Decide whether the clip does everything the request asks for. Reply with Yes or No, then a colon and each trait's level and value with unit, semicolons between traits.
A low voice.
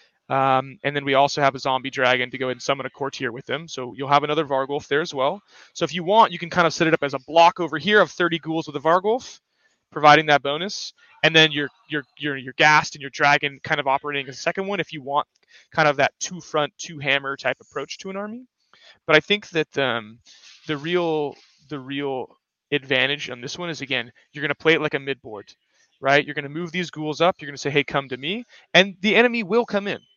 No: medium, 150 Hz